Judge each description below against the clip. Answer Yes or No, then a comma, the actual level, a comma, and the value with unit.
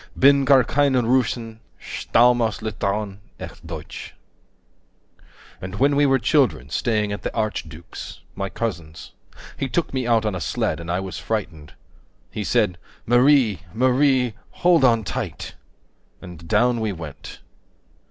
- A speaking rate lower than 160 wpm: Yes, average, 140 wpm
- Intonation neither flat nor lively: No, wide, 5.8 semitones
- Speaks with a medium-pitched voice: No, low, 110 Hz